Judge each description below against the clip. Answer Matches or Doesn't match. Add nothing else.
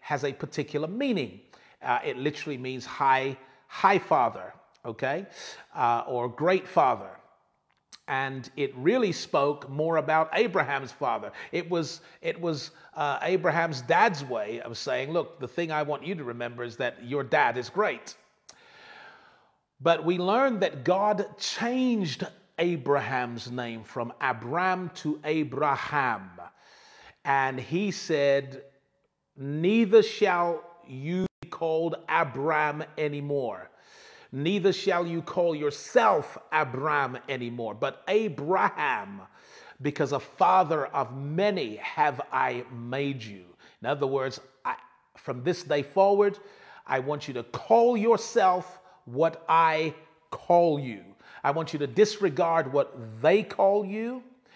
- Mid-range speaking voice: Matches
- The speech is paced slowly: Matches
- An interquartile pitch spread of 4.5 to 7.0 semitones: Matches